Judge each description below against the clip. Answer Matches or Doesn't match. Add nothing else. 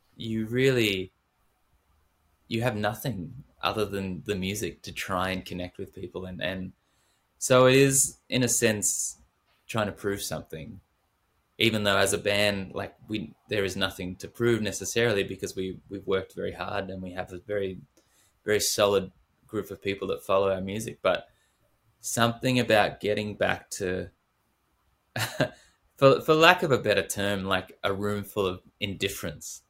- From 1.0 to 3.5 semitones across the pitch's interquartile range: Matches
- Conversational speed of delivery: Matches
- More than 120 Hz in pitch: Doesn't match